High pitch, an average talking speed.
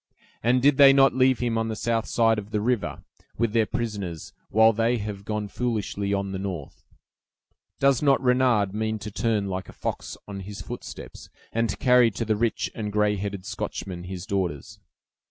No: low, 110 Hz; average, 190 wpm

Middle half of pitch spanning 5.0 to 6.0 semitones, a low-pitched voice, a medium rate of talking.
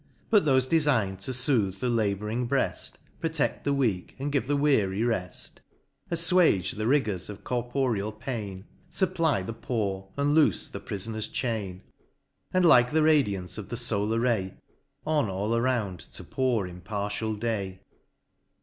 Yes: wide, 5.6 semitones; low, 115 Hz; average, 145 wpm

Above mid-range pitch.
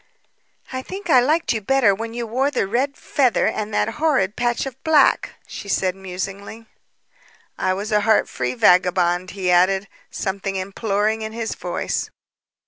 Yes: high, 215 Hz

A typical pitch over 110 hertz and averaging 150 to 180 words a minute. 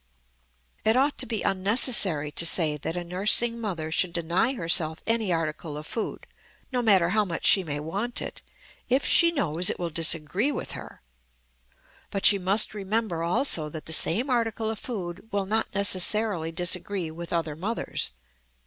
Yes: medium, 185 Hz; average, 165 wpm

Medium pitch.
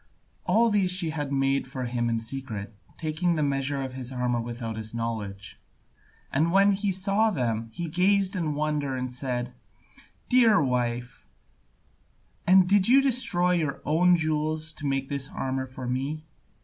Yes: medium, 145 Hz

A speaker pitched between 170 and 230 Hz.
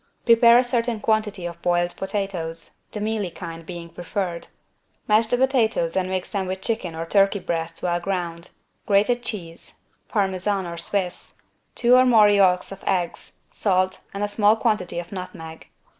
Yes: high, 190 Hz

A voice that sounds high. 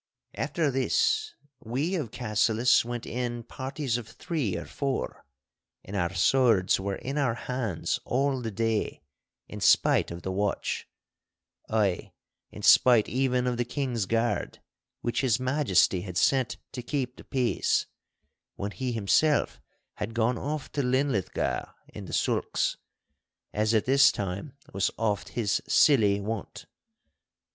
No: low, 120 Hz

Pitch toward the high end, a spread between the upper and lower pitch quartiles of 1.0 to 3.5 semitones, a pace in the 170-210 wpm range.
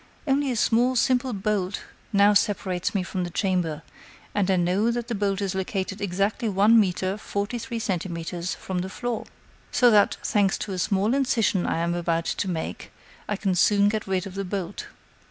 Yes: high, 200 Hz; average, 2.9 semitones; average, 190 wpm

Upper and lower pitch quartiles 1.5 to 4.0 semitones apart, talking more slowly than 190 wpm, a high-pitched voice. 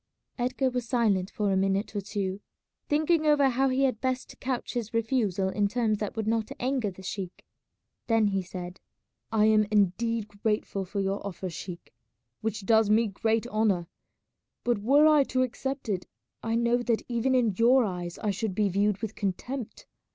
Yes: average, 3.7 semitones; average, 180 wpm; high, 220 Hz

